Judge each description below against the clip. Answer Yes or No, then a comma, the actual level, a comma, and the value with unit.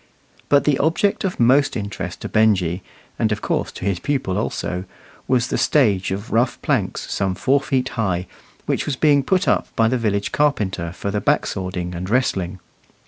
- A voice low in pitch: Yes, low, 110 Hz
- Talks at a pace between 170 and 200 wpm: Yes, average, 185 wpm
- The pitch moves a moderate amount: No, wide, 6.2 semitones